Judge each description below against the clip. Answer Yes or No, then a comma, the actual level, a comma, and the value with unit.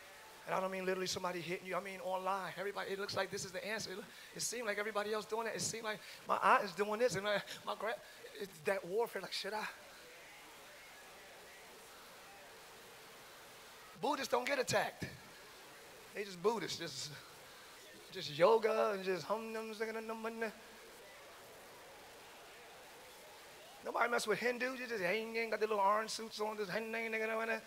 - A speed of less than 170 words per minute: Yes, average, 160 wpm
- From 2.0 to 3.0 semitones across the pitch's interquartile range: Yes, narrow, 2.6 semitones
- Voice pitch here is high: Yes, high, 210 Hz